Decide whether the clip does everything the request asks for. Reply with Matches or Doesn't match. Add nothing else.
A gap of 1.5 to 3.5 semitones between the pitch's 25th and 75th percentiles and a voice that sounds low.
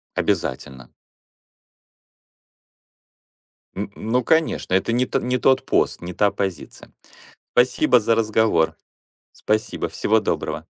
Doesn't match